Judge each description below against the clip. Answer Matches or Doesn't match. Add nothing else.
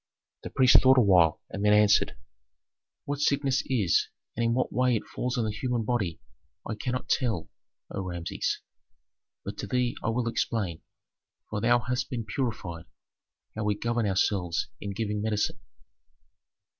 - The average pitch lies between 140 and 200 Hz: Doesn't match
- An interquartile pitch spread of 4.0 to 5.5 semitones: Doesn't match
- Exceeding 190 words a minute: Doesn't match